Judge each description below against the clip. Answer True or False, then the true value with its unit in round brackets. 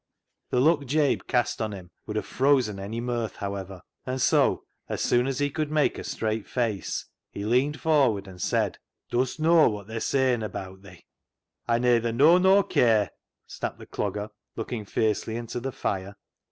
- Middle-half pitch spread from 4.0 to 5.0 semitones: True (4.4 semitones)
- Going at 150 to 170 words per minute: False (195 wpm)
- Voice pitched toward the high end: False (120 Hz)